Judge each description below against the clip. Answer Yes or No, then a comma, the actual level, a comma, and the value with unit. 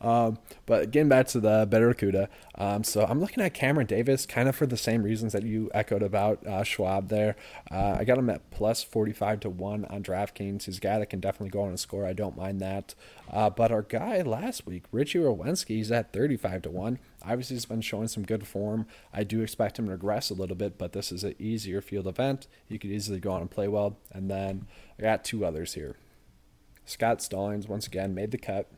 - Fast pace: Yes, fast, 230 wpm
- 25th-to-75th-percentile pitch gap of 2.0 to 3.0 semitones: Yes, narrow, 2.5 semitones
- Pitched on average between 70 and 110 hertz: Yes, low, 105 Hz